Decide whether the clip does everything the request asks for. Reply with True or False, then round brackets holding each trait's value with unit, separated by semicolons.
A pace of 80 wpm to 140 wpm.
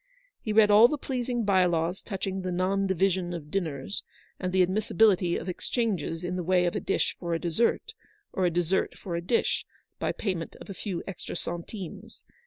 False (195 wpm)